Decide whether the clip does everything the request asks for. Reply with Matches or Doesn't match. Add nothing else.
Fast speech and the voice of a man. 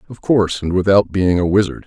Matches